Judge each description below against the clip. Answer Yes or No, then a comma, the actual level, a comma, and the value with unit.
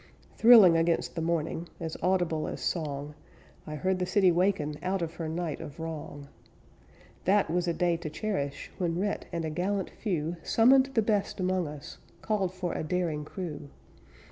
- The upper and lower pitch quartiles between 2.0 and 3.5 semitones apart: Yes, average, 3.1 semitones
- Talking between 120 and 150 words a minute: No, average, 170 wpm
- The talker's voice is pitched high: No, medium, 175 Hz